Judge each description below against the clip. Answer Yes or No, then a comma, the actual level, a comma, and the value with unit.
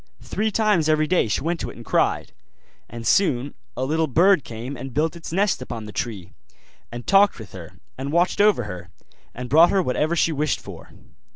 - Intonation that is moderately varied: No, wide, 6.3 semitones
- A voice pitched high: No, medium, 150 Hz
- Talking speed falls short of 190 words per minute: No, average, 200 wpm